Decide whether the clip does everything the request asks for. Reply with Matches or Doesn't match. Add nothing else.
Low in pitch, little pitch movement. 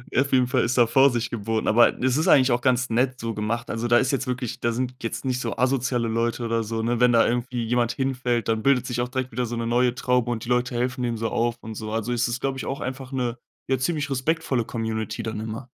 Matches